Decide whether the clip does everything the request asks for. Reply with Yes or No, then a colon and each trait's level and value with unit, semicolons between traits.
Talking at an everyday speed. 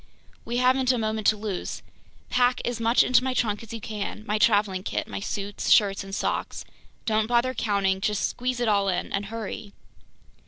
Yes: average, 185 wpm